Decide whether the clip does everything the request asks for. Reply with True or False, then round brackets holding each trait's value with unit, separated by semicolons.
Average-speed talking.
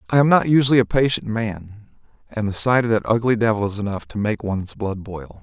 False (230 wpm)